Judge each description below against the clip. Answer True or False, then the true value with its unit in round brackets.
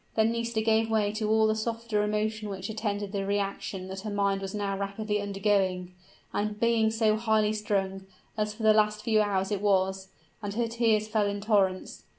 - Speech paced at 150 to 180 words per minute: False (190 wpm)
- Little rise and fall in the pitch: True (1.7 semitones)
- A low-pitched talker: False (210 Hz)